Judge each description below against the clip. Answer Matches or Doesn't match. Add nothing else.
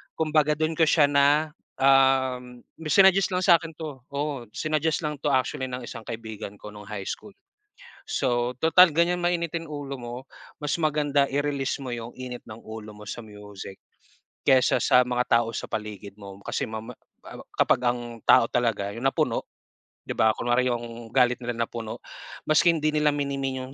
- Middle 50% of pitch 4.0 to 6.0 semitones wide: Matches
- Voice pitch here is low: Matches